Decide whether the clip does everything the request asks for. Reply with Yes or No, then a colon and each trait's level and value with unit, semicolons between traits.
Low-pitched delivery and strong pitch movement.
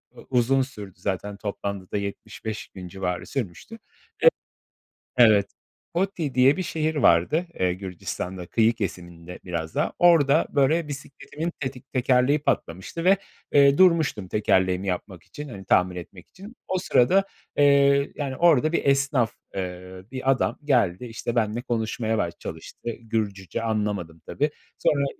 Yes: low, 115 Hz; wide, 6.9 semitones